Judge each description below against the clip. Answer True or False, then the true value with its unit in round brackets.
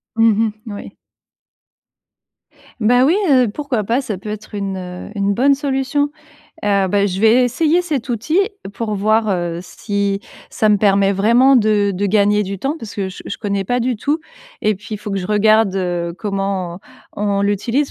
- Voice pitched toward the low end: False (210 Hz)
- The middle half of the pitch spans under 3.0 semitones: False (3.7 semitones)